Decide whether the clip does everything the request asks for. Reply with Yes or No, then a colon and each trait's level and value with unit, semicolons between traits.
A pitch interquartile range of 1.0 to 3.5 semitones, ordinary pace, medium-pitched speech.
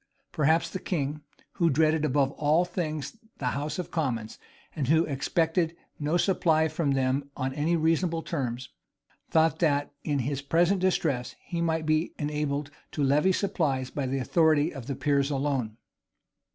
Yes: average, 2.9 semitones; average, 155 wpm; medium, 150 Hz